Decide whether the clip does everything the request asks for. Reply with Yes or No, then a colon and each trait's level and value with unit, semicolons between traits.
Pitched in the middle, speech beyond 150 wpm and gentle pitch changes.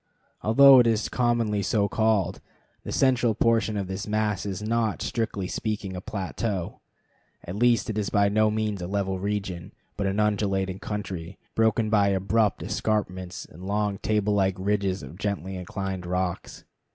No: low, 100 Hz; average, 160 wpm; narrow, 2.3 semitones